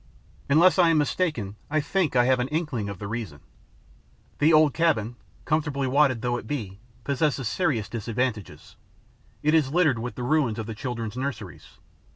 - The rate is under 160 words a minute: No, average, 170 wpm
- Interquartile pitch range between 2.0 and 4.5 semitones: No, average, 5.1 semitones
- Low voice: Yes, low, 130 Hz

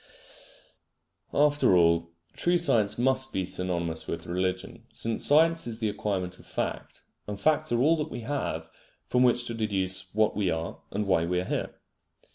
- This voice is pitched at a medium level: No, low, 105 Hz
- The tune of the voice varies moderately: No, wide, 6.1 semitones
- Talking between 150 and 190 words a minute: Yes, average, 170 wpm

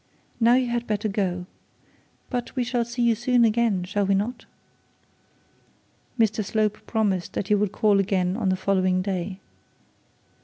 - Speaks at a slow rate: No, average, 155 wpm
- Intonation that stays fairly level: No, average, 3.6 semitones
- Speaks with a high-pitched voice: Yes, high, 210 Hz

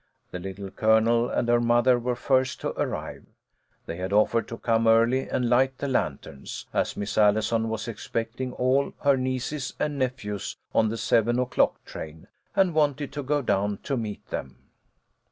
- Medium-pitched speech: No, low, 120 Hz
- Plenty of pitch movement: No, average, 3.2 semitones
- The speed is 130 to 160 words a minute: No, average, 170 wpm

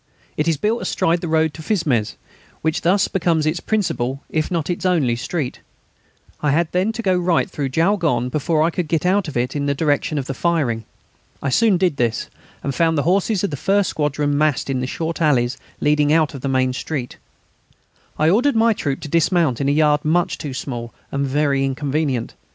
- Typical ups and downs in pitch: Yes, average, 4.0 semitones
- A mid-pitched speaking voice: Yes, medium, 155 Hz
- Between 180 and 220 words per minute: Yes, fast, 205 wpm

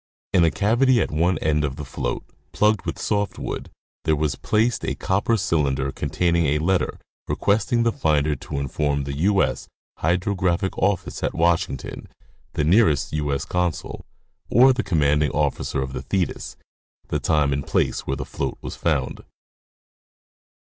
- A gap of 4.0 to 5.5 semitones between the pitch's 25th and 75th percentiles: Yes, average, 5.2 semitones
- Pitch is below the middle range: Yes, very low, 80 Hz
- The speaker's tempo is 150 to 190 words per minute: Yes, average, 160 wpm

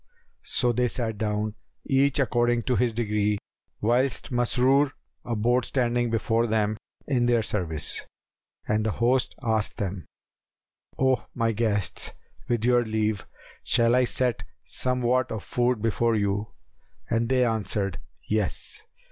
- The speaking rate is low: Yes, slow, 130 wpm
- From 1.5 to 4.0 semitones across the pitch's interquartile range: Yes, narrow, 2.5 semitones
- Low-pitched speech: Yes, low, 115 Hz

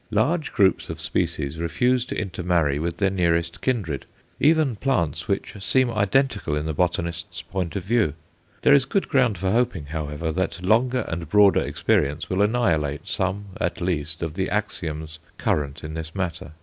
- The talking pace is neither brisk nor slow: Yes, average, 170 wpm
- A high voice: No, very low, 90 Hz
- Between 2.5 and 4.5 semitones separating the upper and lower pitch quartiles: No, wide, 5.5 semitones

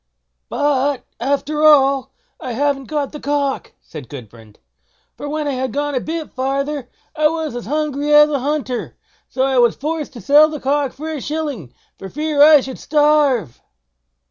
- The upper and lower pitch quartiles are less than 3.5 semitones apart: Yes, narrow, 2.6 semitones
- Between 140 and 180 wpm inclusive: Yes, average, 170 wpm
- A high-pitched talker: Yes, very high, 285 Hz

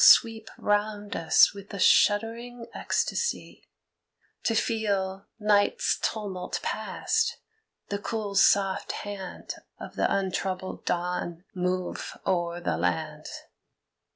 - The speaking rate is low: Yes, slow, 100 wpm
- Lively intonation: No, average, 2.8 semitones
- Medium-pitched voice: No, high, 200 Hz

